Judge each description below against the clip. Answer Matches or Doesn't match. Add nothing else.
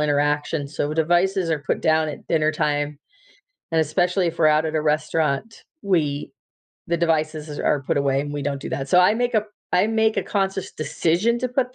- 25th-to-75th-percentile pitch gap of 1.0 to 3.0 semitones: Doesn't match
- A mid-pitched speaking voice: Matches